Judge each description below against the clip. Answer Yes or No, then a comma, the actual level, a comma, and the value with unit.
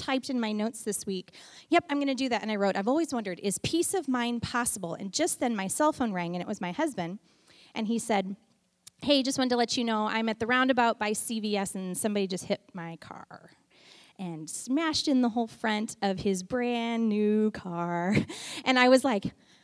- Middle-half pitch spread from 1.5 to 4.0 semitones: No, average, 4.5 semitones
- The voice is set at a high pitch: Yes, high, 220 Hz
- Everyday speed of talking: No, fast, 215 wpm